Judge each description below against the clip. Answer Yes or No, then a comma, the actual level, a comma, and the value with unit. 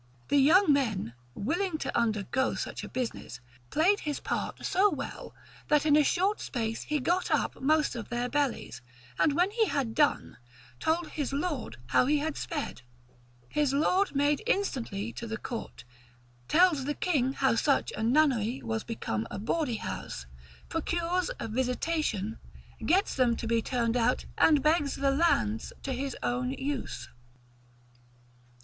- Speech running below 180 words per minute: Yes, average, 155 wpm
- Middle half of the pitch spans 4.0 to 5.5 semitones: Yes, average, 5.1 semitones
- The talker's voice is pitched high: Yes, very high, 275 Hz